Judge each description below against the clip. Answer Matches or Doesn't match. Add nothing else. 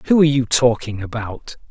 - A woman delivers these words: Doesn't match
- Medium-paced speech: Matches